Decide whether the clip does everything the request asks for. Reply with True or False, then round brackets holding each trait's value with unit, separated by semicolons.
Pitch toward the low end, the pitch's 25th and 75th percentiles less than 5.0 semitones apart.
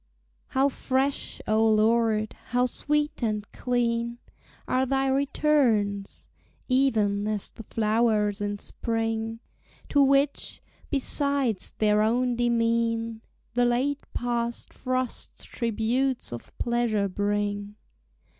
False (235 Hz; 3.2 semitones)